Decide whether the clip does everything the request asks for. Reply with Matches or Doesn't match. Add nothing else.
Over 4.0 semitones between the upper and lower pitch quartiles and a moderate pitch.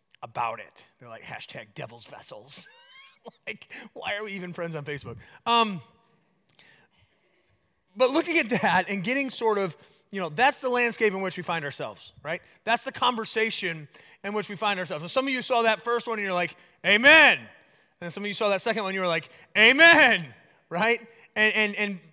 Doesn't match